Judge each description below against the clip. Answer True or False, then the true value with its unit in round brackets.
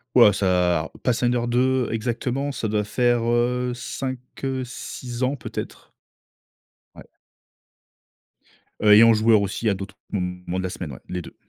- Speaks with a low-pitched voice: True (115 Hz)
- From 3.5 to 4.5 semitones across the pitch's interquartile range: True (4.1 semitones)